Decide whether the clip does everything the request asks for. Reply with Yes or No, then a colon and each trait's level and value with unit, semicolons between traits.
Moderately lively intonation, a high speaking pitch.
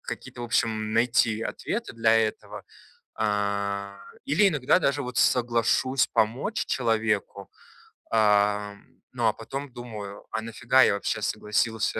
No: average, 3.0 semitones; low, 110 Hz